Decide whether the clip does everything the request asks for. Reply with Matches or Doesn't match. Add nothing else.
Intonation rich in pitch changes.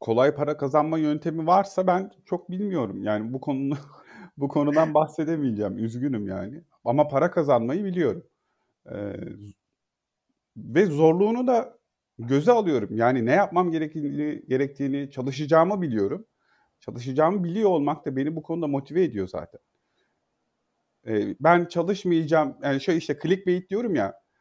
Doesn't match